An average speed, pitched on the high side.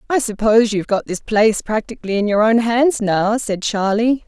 Yes: average, 195 wpm; high, 220 Hz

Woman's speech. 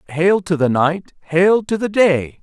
No: male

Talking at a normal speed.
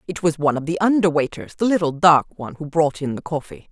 No: fast, 225 wpm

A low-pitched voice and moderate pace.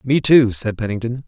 Yes: low, 125 Hz; average, 190 wpm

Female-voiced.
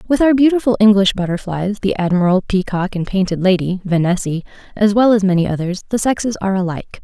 Yes: female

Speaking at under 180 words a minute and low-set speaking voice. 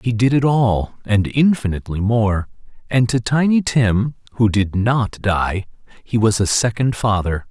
Yes: average, 160 wpm; low, 115 Hz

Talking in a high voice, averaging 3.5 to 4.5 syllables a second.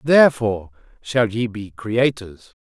No: low, 115 Hz; 4.2 syllables/s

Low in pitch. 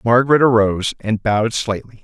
Yes: low, 110 Hz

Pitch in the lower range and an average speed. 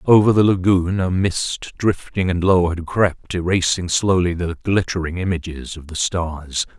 Yes: very low, 90 Hz; average, 160 wpm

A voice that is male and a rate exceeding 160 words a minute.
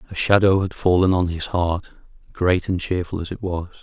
Yes: male; fast, 205 wpm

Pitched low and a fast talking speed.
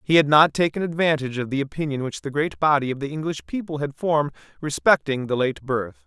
No: medium, 145 Hz; fast, 220 wpm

